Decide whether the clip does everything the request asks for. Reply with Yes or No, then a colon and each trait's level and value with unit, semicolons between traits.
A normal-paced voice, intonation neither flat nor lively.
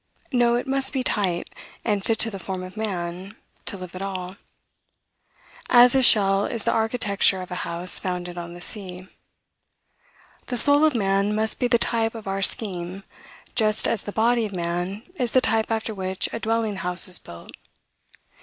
Yes: average, 180 wpm; average, 3.8 semitones